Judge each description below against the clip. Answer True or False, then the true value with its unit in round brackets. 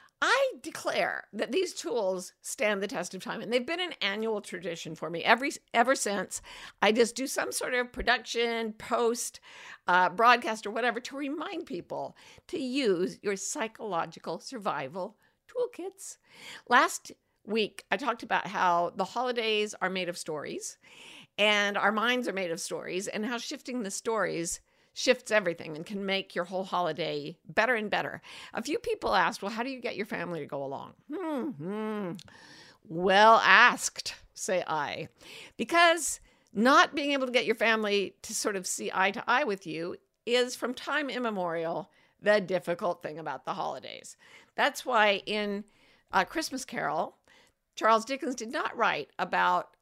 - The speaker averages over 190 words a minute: False (165 wpm)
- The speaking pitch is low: False (220 Hz)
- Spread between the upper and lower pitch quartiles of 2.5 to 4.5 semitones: False (5.3 semitones)